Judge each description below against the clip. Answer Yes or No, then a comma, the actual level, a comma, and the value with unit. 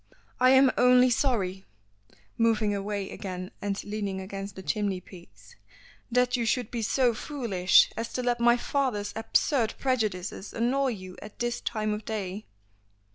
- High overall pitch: Yes, high, 215 Hz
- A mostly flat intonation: No, average, 3.9 semitones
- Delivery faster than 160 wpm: No, average, 150 wpm